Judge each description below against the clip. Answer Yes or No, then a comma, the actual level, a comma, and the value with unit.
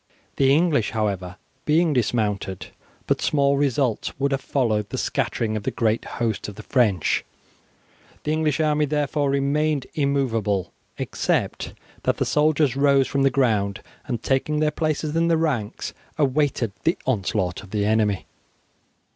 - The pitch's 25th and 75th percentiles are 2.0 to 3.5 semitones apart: No, wide, 5.6 semitones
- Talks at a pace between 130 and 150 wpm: Yes, average, 145 wpm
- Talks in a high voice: No, low, 135 Hz